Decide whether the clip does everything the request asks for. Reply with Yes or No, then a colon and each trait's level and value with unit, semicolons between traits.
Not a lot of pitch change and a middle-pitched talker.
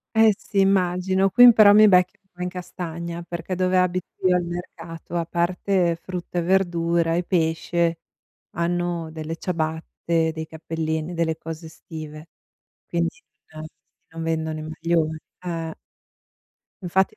Yes: narrow, 1.9 semitones; medium, 170 Hz